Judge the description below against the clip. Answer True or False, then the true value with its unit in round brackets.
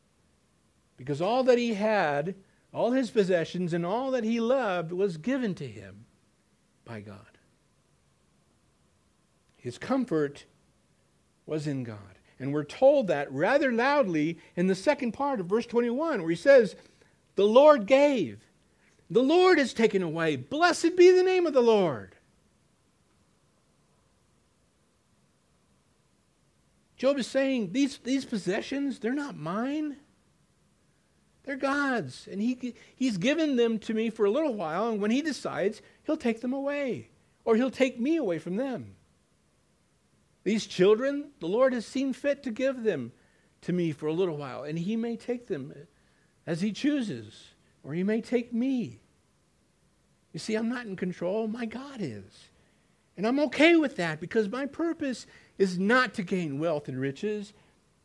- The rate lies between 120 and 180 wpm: True (150 wpm)